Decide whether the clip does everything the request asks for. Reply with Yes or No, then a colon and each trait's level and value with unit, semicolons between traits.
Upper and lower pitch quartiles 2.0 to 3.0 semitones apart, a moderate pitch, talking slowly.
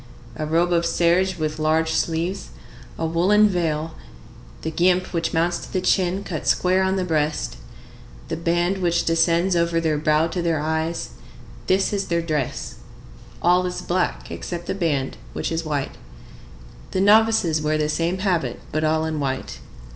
No: narrow, 2.5 semitones; medium, 170 Hz; average, 165 wpm